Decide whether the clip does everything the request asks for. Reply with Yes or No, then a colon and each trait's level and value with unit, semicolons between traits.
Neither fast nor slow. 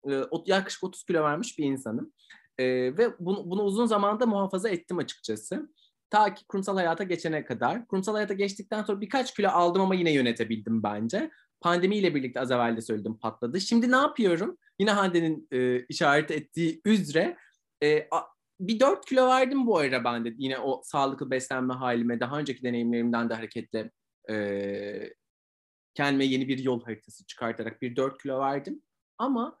No: fast, 160 wpm